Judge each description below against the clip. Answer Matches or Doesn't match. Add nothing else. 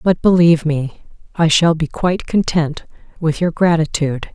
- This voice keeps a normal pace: Matches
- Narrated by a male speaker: Doesn't match